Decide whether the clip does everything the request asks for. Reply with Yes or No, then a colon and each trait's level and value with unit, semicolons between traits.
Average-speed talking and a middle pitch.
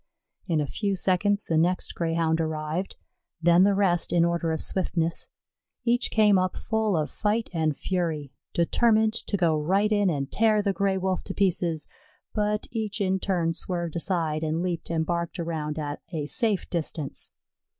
Yes: average, 170 wpm; medium, 175 Hz